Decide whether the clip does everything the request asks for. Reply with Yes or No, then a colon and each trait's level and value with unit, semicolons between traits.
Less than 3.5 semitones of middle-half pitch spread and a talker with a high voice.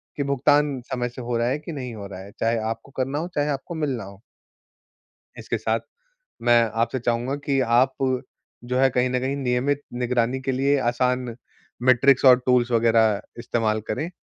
No: narrow, 2.5 semitones; low, 125 Hz